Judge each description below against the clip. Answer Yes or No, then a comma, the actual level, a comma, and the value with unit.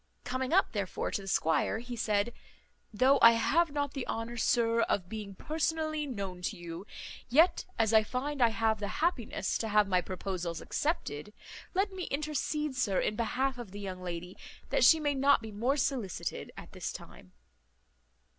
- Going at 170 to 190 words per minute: Yes, average, 175 wpm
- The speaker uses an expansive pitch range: Yes, wide, 6.0 semitones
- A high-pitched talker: Yes, high, 230 Hz